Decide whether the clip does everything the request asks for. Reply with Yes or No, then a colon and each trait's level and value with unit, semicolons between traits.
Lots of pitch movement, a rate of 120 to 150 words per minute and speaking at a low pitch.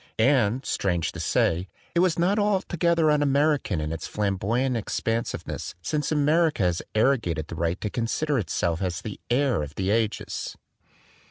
No: wide, 8.3 semitones; average, 160 wpm; low, 115 Hz